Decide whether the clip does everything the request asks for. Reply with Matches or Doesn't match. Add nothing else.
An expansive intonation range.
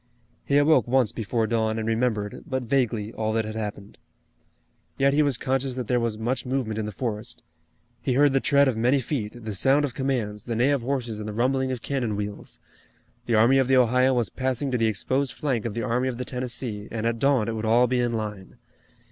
Doesn't match